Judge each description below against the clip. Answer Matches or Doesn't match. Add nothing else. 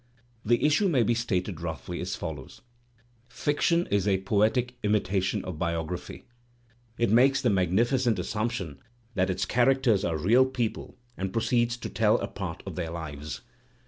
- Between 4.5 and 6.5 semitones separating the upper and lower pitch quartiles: Matches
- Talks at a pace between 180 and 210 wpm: Doesn't match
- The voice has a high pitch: Doesn't match